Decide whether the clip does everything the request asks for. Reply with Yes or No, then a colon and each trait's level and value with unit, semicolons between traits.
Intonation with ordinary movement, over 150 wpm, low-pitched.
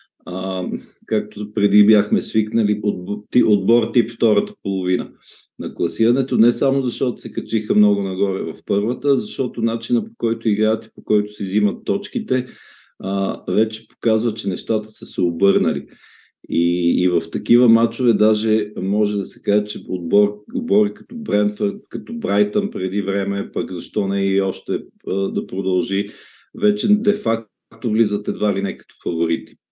No: average, 3.2 semitones; average, 145 wpm; low, 105 Hz